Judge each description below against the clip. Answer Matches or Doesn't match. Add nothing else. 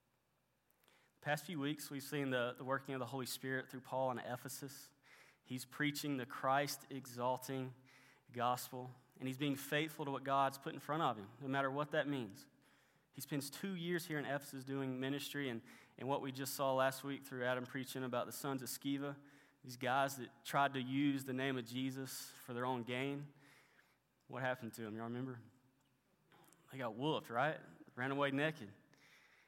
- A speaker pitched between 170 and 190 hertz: Doesn't match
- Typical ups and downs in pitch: Doesn't match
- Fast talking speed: Doesn't match